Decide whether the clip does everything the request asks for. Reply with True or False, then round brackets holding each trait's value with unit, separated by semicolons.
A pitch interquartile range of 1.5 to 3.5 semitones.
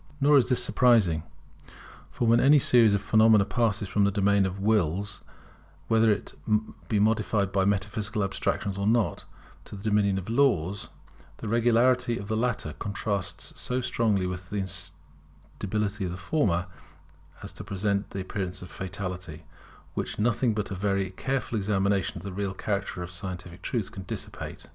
True (2.7 semitones)